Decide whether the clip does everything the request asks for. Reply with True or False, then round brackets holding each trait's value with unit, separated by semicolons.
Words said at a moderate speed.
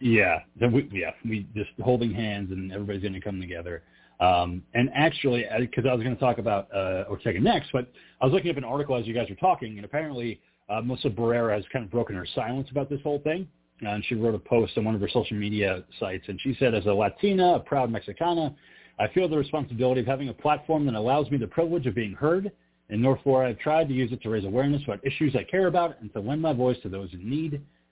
False (255 wpm)